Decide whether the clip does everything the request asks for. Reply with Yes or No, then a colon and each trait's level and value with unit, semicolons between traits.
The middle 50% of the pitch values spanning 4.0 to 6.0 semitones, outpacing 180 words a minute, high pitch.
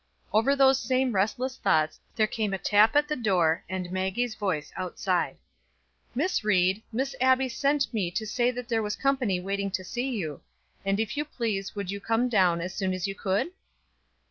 Yes: average, 4.9 semitones; average, 190 wpm; high, 215 Hz